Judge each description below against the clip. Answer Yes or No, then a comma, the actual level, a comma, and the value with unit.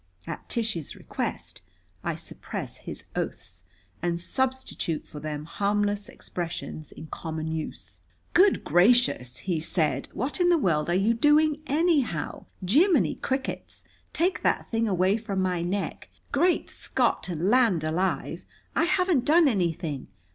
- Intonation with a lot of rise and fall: Yes, wide, 8.2 semitones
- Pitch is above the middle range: Yes, high, 200 Hz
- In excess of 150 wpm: No, slow, 135 wpm